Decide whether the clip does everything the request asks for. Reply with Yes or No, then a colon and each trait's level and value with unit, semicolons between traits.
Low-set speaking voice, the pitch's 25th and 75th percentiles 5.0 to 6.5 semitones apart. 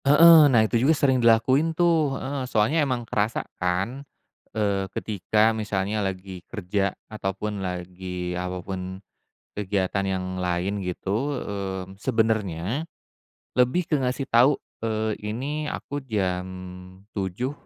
Yes: low, 105 Hz; wide, 5.5 semitones